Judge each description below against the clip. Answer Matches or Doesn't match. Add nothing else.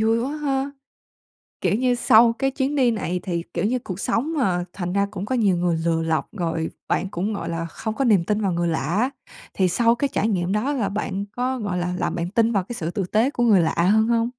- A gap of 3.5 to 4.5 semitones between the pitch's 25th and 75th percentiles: Doesn't match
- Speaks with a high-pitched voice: Matches